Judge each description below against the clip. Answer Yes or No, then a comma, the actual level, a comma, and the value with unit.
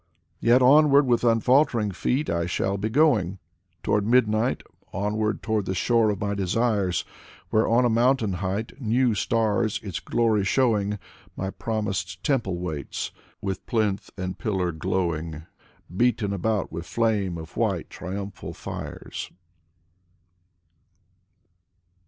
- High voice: No, low, 105 Hz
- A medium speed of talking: No, slow, 130 wpm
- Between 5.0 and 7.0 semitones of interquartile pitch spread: No, average, 3.7 semitones